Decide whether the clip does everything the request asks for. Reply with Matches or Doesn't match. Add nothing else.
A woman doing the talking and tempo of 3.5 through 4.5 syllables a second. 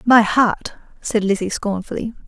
Matches